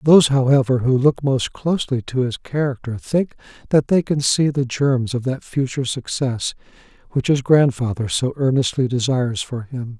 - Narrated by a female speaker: No, male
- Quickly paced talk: No, average, 170 wpm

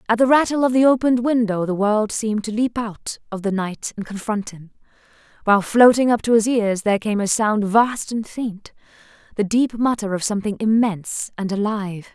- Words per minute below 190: No, average, 200 wpm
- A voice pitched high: Yes, high, 220 Hz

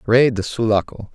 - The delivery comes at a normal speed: Yes, average, 155 wpm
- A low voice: Yes, low, 115 Hz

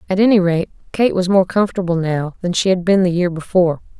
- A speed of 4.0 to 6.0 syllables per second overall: No, 6.2 syllables/s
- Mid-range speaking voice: Yes, medium, 180 Hz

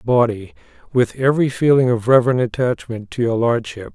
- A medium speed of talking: Yes, average, 150 wpm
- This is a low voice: Yes, low, 120 Hz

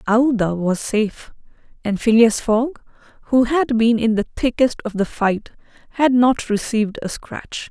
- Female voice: Yes, female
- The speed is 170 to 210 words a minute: No, average, 155 wpm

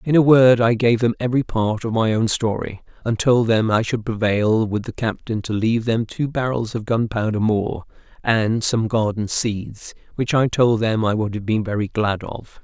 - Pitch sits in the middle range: No, low, 110 Hz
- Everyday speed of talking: No, fast, 210 wpm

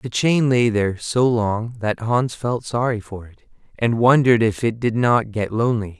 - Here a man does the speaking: Yes, male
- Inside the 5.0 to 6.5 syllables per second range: No, 4.6 syllables/s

